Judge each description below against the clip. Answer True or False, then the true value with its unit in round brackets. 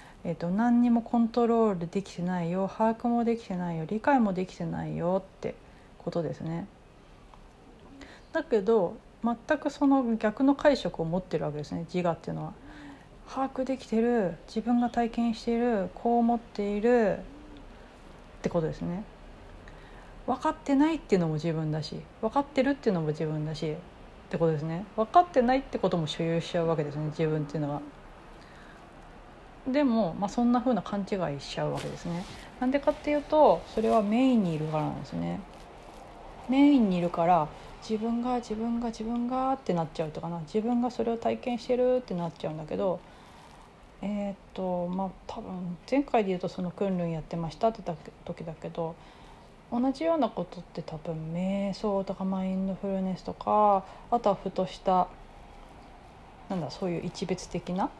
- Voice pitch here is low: False (200 Hz)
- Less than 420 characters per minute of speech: True (365 characters per minute)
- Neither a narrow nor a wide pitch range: False (5.7 semitones)